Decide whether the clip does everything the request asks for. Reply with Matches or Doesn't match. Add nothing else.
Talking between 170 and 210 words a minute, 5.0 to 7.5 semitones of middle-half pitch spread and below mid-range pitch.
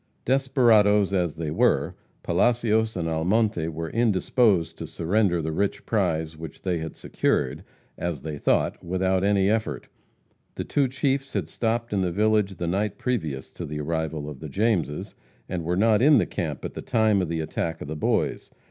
Matches